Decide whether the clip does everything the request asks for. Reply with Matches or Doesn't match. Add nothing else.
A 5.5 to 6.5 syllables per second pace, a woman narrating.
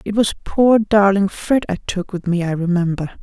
Doesn't match